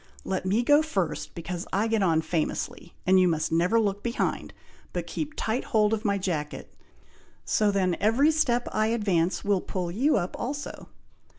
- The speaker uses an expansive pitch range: No, average, 4.4 semitones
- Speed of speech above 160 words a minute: Yes, average, 175 wpm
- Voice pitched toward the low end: No, high, 200 Hz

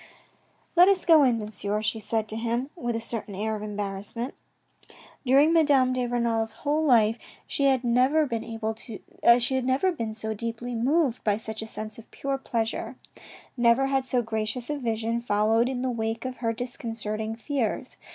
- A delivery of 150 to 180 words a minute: Yes, average, 170 wpm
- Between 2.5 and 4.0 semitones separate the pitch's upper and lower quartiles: Yes, average, 2.9 semitones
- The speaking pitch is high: Yes, high, 235 Hz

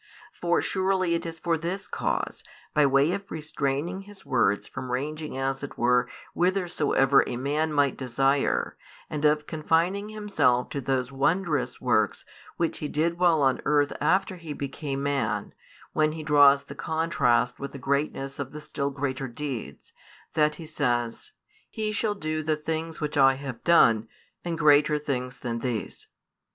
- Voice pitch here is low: No, medium, 150 Hz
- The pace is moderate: Yes, average, 160 wpm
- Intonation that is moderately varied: Yes, average, 3.5 semitones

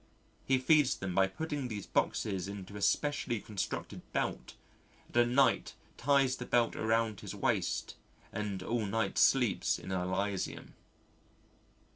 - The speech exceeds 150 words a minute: No, slow, 135 wpm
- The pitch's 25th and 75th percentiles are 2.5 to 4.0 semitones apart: No, average, 4.5 semitones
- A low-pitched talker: Yes, low, 110 Hz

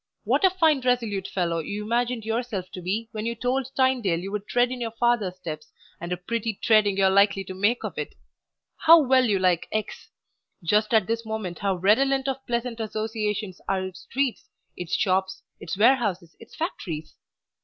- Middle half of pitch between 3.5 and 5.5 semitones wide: Yes, average, 4.3 semitones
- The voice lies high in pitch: Yes, high, 215 Hz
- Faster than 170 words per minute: Yes, average, 185 wpm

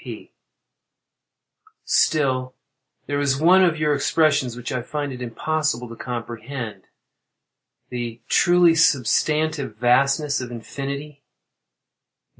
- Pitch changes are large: No, average, 3.8 semitones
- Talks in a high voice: No, medium, 140 Hz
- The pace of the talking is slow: Yes, slow, 95 wpm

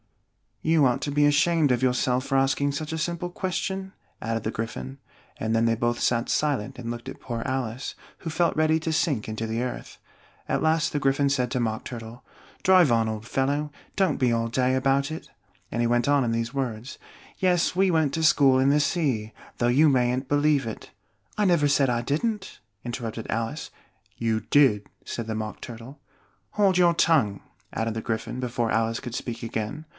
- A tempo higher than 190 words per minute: Yes, average, 200 wpm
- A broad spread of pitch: No, average, 4.7 semitones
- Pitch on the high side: No, low, 130 Hz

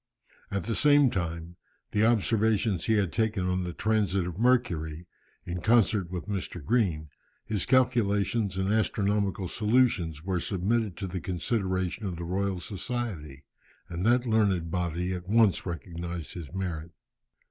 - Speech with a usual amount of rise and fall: Yes, average, 4.0 semitones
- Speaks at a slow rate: No, average, 145 wpm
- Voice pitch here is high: No, very low, 95 Hz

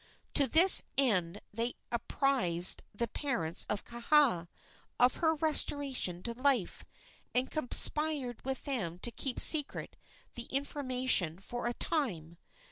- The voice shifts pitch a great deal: Yes, wide, 5.8 semitones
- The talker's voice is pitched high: Yes, very high, 250 Hz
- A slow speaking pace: Yes, slow, 125 wpm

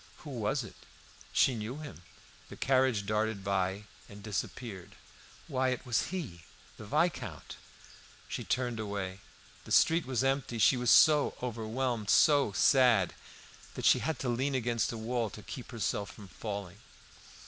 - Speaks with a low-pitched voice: Yes, low, 115 Hz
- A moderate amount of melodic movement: Yes, average, 4.3 semitones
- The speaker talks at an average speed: Yes, average, 150 wpm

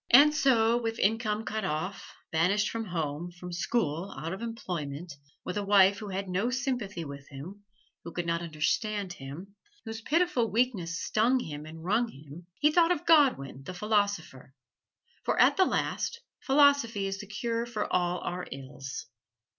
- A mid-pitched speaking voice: No, high, 200 Hz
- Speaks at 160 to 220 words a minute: Yes, average, 165 wpm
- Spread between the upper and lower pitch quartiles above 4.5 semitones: Yes, wide, 5.5 semitones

